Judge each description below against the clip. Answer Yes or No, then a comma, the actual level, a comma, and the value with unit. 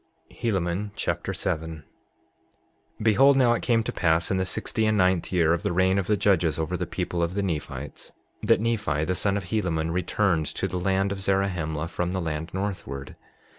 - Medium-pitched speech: No, very low, 90 Hz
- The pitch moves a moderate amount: Yes, average, 3.5 semitones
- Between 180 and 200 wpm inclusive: Yes, average, 195 wpm